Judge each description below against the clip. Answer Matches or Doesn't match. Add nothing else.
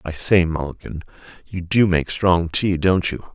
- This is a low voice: Matches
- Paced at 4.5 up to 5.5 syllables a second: Matches